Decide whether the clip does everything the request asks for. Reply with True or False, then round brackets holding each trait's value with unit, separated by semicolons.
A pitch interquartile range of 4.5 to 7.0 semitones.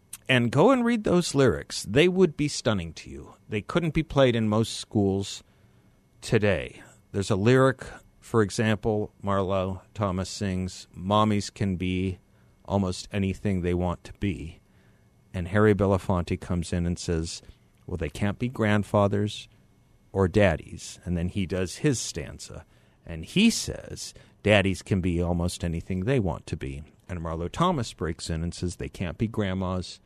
False (3.4 semitones)